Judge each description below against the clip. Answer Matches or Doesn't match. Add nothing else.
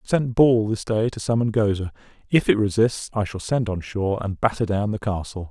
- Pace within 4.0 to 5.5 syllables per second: Doesn't match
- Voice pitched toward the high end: Doesn't match